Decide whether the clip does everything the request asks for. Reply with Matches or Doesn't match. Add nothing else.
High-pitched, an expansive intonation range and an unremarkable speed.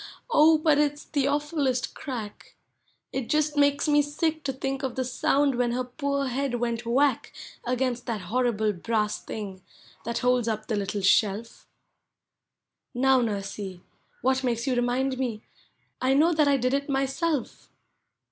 Doesn't match